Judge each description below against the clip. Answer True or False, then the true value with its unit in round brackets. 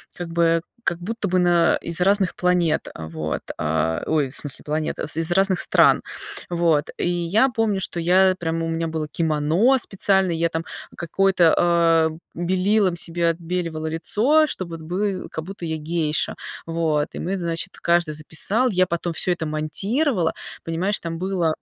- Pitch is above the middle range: False (170 Hz)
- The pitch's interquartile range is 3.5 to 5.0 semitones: False (2.6 semitones)